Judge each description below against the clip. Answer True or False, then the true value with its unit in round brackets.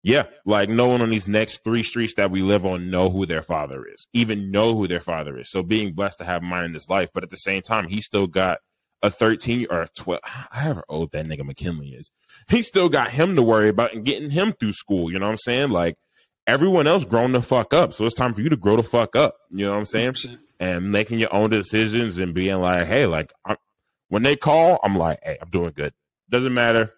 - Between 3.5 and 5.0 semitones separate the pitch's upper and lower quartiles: True (4.3 semitones)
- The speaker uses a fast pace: True (255 wpm)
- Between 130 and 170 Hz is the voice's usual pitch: False (105 Hz)